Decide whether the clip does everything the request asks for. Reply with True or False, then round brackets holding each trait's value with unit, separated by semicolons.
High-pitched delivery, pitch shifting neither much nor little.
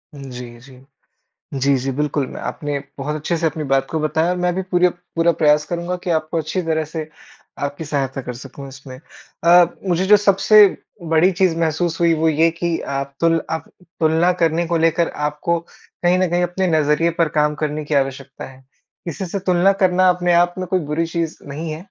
False (160 Hz; 3.0 semitones)